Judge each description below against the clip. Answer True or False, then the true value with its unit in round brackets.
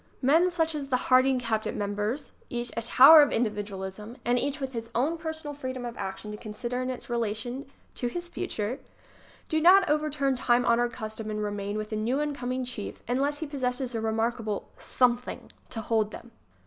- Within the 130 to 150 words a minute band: False (190 wpm)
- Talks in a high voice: True (245 Hz)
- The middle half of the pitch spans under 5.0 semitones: True (4.1 semitones)